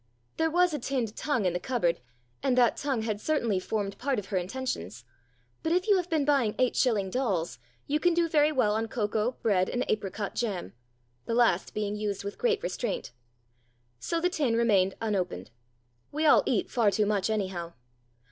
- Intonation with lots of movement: Yes, wide, 6.3 semitones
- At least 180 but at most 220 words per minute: Yes, average, 185 wpm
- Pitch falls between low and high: No, high, 225 Hz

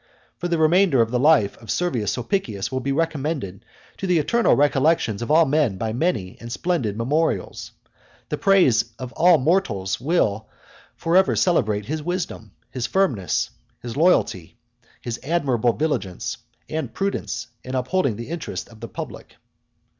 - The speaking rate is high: No, average, 155 wpm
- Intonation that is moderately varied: No, wide, 6.7 semitones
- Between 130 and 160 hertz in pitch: Yes, low, 135 Hz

